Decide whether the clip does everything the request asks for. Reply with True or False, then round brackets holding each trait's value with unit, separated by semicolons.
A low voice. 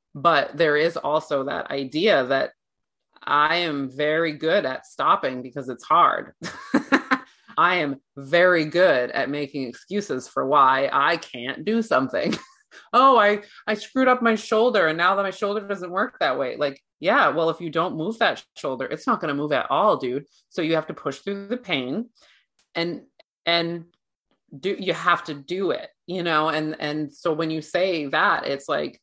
False (170 Hz)